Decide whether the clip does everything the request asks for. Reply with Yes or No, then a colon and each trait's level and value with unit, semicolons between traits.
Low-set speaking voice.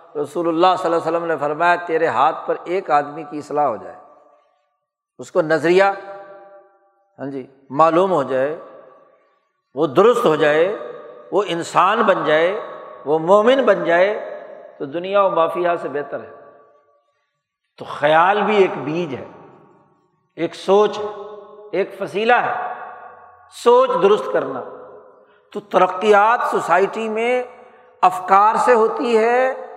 No: high, 195 Hz